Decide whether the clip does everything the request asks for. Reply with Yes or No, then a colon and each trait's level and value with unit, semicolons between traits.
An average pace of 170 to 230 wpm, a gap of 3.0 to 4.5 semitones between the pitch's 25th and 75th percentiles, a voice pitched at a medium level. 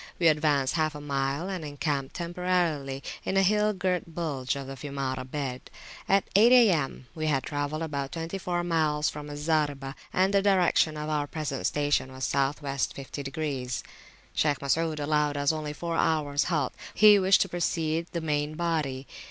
Yes: average, 175 wpm; average, 3.3 semitones; medium, 150 Hz